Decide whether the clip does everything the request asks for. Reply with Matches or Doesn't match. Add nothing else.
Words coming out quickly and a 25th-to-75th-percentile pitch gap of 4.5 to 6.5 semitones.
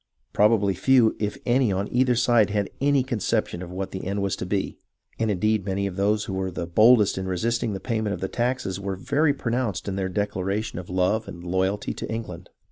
Doesn't match